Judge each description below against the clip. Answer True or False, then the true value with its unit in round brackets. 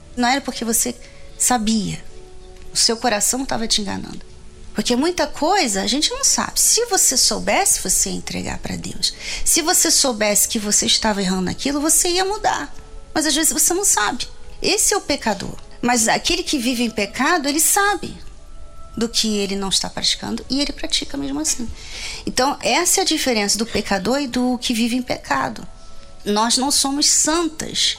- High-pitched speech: True (260 Hz)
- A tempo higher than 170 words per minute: True (180 wpm)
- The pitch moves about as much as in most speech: False (6.2 semitones)